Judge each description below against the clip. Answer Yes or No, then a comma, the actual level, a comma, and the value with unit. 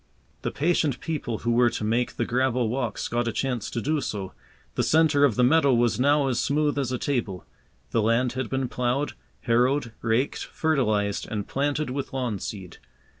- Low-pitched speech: Yes, low, 125 Hz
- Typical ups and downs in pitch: Yes, average, 3.4 semitones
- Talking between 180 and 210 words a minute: Yes, average, 185 wpm